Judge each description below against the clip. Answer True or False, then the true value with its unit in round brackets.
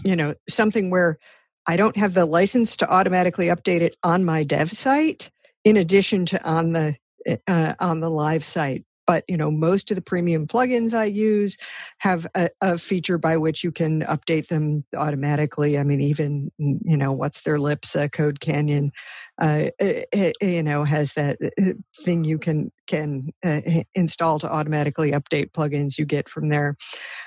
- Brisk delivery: False (175 wpm)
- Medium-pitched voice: True (165 Hz)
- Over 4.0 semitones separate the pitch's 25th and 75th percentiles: False (3.6 semitones)